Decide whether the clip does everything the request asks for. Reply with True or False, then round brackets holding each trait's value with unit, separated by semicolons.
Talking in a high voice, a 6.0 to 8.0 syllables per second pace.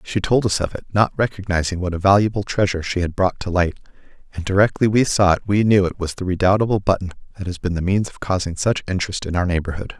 False (95 Hz; 6.5 syllables/s)